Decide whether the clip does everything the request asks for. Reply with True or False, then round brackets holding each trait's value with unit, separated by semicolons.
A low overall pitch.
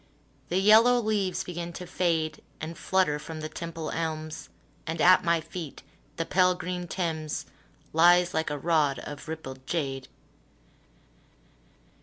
False (165 Hz)